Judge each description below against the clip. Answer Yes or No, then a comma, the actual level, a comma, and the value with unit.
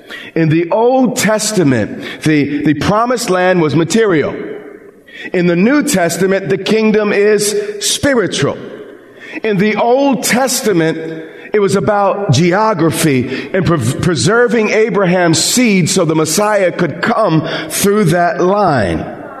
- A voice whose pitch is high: Yes, high, 195 Hz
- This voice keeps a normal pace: No, slow, 120 wpm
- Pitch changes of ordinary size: Yes, average, 4.6 semitones